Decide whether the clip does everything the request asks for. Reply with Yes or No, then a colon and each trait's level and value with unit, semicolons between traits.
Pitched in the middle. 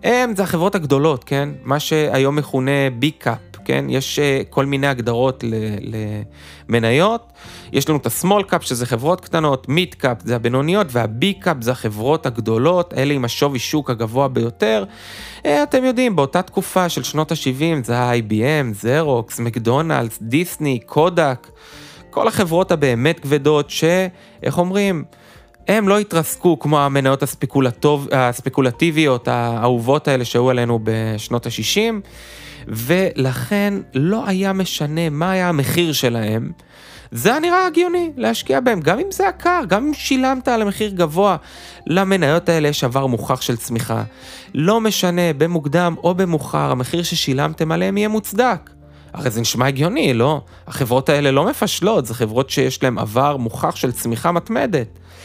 Yes: medium, 145 Hz